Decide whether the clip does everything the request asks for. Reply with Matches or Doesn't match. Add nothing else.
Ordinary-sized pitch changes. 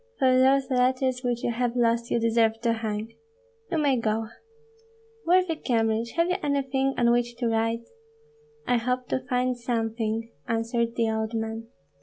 Doesn't match